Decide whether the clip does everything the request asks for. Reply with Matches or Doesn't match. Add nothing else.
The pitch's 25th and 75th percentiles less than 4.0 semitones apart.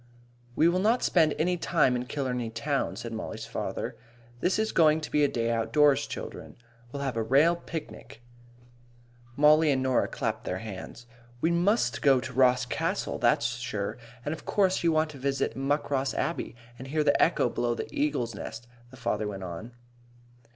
Doesn't match